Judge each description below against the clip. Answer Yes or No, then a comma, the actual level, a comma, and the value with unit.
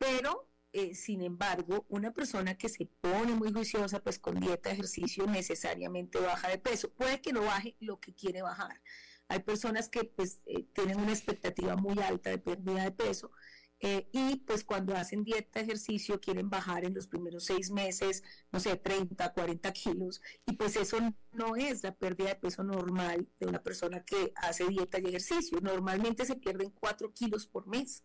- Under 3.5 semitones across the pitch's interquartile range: Yes, average, 3.1 semitones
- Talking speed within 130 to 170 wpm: No, average, 185 wpm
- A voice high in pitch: Yes, high, 195 Hz